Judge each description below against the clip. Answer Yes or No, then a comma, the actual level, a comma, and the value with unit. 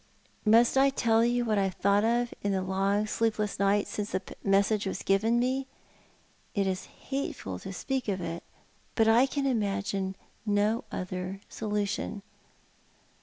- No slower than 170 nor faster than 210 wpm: No, average, 155 wpm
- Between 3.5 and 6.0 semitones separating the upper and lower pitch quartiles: No, average, 2.9 semitones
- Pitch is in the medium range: No, high, 205 Hz